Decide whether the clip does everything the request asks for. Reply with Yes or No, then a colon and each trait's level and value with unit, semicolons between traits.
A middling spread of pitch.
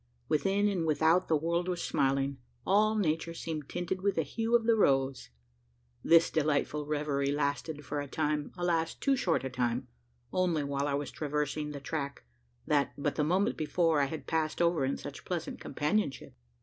Yes: average, 3.5 semitones